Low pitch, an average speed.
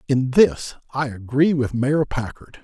Yes: low, 130 Hz; average, 160 wpm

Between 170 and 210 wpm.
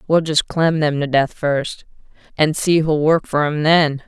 Yes: fast, 205 wpm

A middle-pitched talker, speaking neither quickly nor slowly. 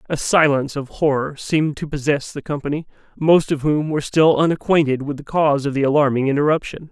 Yes: medium, 145 Hz; average, 190 wpm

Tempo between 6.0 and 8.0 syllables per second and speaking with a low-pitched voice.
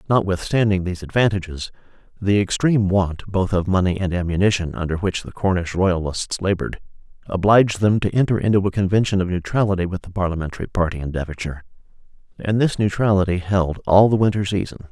Yes: 6.2 syllables/s; very low, 95 Hz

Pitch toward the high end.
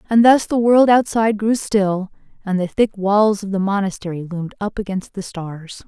Yes: high, 200 Hz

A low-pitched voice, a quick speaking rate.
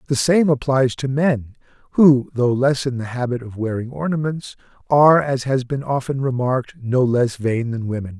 No: low, 130 Hz; average, 185 wpm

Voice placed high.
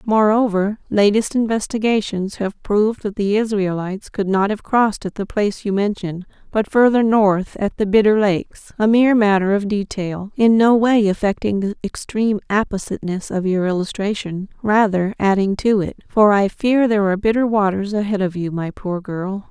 Yes: high, 205 Hz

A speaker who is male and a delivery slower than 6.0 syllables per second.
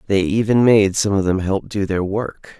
Yes: male; 4.6 syllables/s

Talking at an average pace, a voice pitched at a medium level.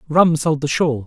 No: fast, 225 wpm; medium, 150 Hz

